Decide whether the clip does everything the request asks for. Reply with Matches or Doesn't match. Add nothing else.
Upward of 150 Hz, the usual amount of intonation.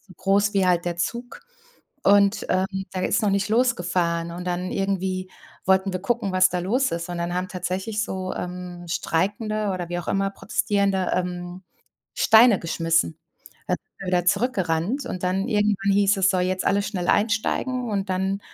Doesn't match